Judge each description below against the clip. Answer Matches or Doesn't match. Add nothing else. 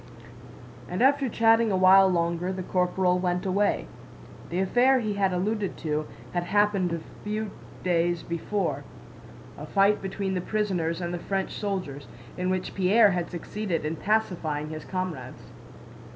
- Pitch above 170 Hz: Matches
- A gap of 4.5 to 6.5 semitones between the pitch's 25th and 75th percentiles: Doesn't match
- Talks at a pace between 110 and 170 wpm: Matches